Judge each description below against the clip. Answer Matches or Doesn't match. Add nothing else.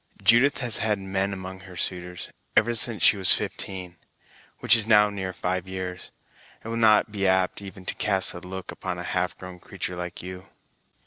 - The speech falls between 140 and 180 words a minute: Doesn't match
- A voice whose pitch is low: Matches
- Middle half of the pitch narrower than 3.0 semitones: Matches